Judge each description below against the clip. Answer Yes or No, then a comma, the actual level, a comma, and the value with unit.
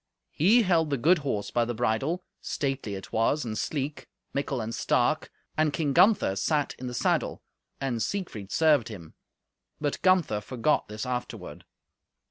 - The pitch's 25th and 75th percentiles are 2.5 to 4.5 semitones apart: No, wide, 5.6 semitones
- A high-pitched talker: No, low, 135 Hz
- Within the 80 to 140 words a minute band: No, average, 155 wpm